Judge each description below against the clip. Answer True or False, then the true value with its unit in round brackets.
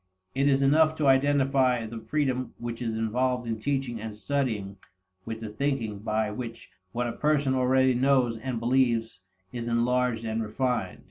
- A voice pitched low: True (125 Hz)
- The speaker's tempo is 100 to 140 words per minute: False (160 wpm)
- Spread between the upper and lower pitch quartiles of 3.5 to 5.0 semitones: False (3.0 semitones)